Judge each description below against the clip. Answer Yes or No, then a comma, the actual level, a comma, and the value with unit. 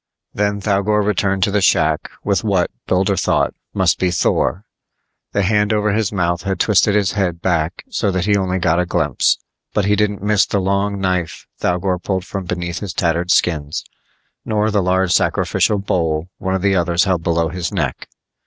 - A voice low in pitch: Yes, very low, 95 Hz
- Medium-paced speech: Yes, average, 185 wpm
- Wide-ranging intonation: No, narrow, 2.5 semitones